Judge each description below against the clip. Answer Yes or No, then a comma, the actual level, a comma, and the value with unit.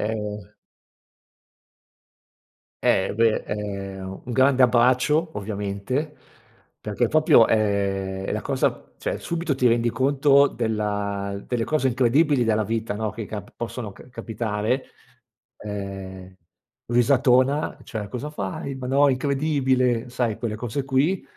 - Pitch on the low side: Yes, low, 115 Hz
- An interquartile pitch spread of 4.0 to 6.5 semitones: Yes, average, 4.3 semitones